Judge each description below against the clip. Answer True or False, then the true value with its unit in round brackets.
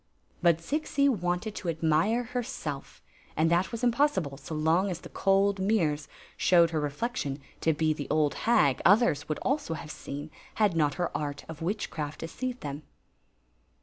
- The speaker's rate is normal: True (150 wpm)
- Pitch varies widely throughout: True (6.1 semitones)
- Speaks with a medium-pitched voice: True (170 Hz)